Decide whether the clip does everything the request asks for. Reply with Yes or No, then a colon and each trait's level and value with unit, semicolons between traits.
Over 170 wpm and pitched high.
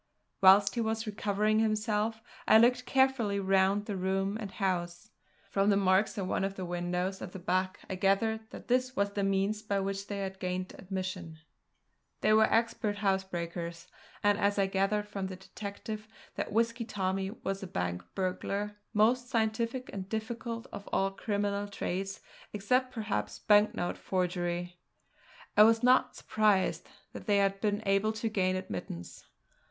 No: average, 160 wpm; high, 200 Hz